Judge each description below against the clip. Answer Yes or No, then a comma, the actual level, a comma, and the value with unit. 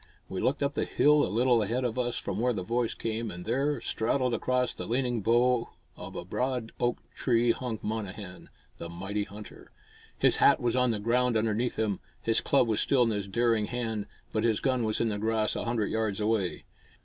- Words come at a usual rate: No, fast, 210 wpm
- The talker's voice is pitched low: Yes, low, 115 Hz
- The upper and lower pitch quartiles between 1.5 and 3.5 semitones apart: Yes, narrow, 2.6 semitones